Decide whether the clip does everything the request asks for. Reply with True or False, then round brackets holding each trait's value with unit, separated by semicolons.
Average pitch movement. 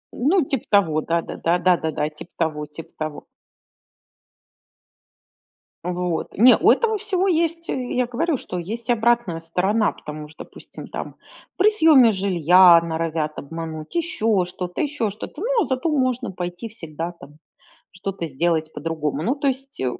False (7.9 semitones)